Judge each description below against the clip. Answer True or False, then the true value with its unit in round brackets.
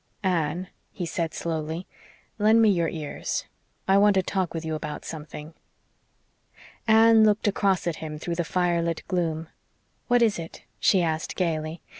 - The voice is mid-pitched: True (170 Hz)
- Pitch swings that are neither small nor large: True (3.5 semitones)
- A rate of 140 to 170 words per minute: True (160 wpm)